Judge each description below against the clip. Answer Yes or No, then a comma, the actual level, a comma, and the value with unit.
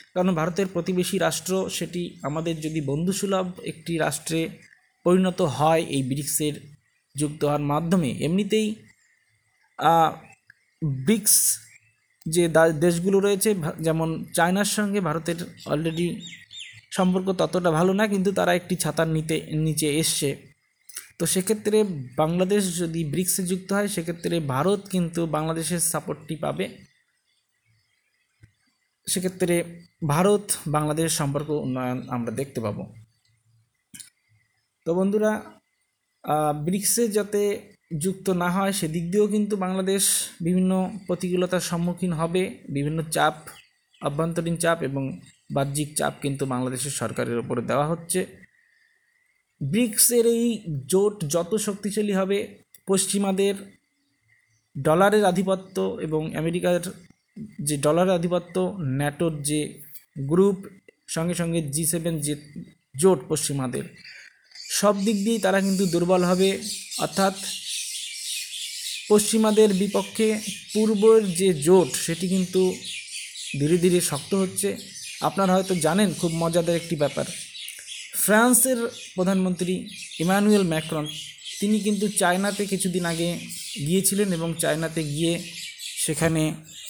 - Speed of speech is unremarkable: Yes, average, 105 wpm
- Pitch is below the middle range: No, medium, 175 Hz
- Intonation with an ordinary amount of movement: Yes, average, 3.9 semitones